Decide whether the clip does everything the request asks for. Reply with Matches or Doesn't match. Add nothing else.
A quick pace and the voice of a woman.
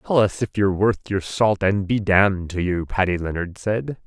Doesn't match